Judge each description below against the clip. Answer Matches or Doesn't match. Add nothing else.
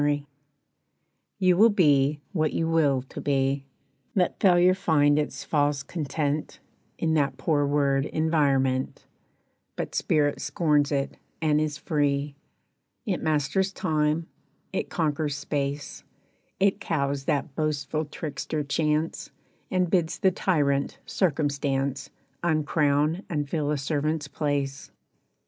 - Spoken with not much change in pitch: Matches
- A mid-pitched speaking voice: Matches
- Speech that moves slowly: Matches